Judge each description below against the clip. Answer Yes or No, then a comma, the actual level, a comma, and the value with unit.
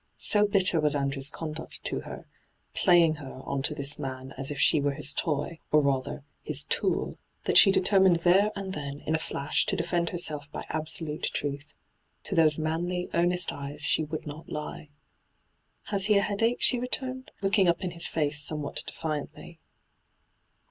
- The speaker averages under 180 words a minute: No, average, 190 wpm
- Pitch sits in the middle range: Yes, medium, 155 Hz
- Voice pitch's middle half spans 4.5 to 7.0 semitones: No, average, 3.7 semitones